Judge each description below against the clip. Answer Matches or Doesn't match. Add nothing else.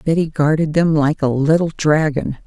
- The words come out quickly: Doesn't match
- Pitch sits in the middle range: Matches